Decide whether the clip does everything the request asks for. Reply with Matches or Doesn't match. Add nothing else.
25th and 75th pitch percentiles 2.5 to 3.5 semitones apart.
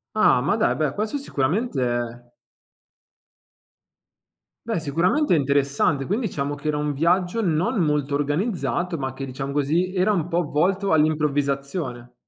Doesn't match